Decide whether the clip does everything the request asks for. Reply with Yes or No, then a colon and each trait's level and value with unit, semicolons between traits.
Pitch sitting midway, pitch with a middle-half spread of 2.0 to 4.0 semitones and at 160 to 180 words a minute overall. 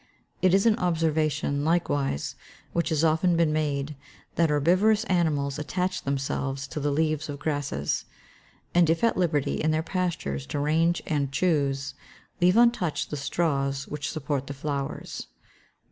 No: medium, 155 Hz; average, 3.5 semitones; average, 145 wpm